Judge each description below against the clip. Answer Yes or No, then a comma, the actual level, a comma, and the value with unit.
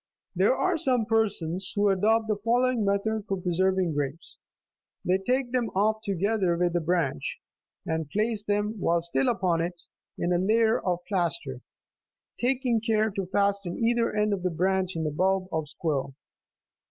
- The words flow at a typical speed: Yes, average, 165 wpm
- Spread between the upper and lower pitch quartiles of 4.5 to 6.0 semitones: No, average, 3.9 semitones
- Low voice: No, high, 195 Hz